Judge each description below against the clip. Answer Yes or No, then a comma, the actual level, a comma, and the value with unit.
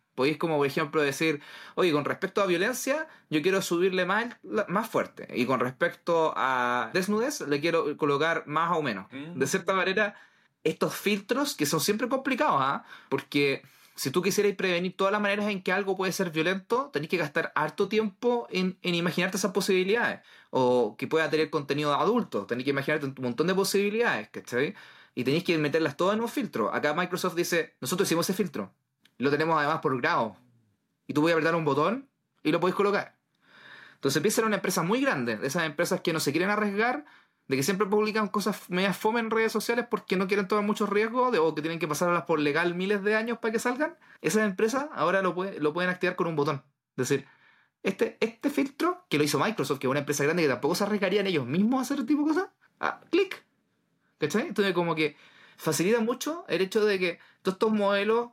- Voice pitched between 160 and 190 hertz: Yes, medium, 185 Hz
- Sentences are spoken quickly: Yes, fast, 210 wpm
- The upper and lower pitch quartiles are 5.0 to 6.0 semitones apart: Yes, wide, 5.5 semitones